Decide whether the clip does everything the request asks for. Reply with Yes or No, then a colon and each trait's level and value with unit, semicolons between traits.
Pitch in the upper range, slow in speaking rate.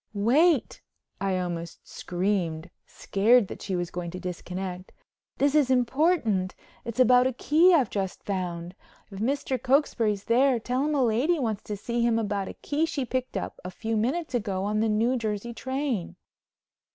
No: high, 225 Hz; average, 170 wpm